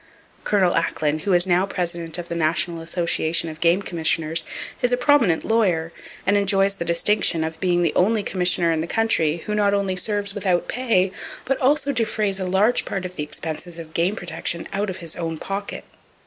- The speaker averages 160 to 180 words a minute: No, average, 190 wpm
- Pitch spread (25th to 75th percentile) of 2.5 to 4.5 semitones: Yes, average, 3.4 semitones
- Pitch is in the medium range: Yes, medium, 180 Hz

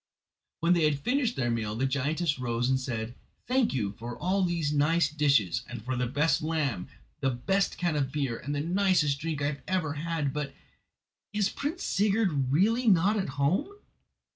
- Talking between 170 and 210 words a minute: Yes, average, 180 wpm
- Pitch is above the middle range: No, medium, 150 Hz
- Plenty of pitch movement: Yes, wide, 5.7 semitones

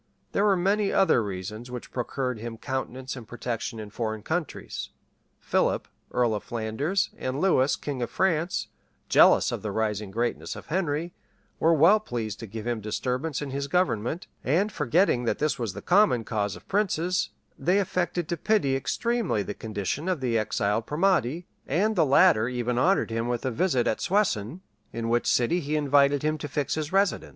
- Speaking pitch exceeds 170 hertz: No, low, 135 Hz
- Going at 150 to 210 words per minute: Yes, average, 180 wpm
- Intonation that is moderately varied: No, wide, 7.2 semitones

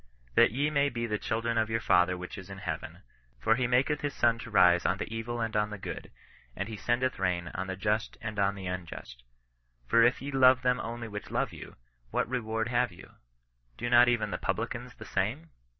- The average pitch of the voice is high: No, low, 110 Hz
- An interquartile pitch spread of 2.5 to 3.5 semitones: No, average, 4.0 semitones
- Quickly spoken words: Yes, fast, 220 wpm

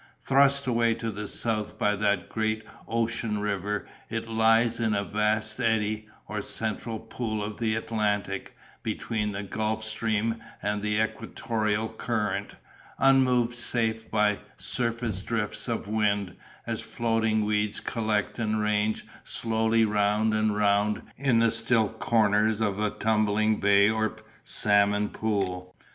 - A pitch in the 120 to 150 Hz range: No, low, 110 Hz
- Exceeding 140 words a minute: No, slow, 135 wpm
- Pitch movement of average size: No, narrow, 1.4 semitones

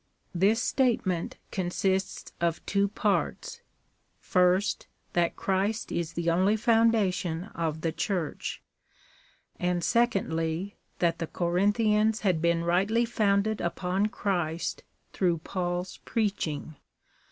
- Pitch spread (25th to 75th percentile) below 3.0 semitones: No, average, 3.5 semitones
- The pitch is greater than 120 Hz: Yes, medium, 185 Hz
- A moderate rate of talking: No, slow, 105 wpm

